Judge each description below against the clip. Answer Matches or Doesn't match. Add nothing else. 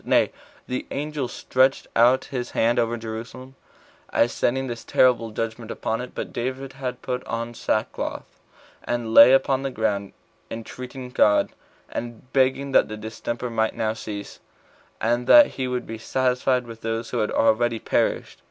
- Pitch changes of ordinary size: Doesn't match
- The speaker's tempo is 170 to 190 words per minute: Doesn't match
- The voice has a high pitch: Doesn't match